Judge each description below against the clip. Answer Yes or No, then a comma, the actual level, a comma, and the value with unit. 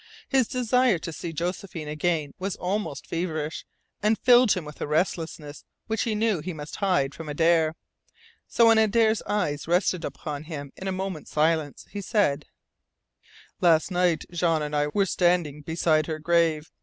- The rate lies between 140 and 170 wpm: Yes, average, 165 wpm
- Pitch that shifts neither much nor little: Yes, average, 4.3 semitones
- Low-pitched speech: No, medium, 170 Hz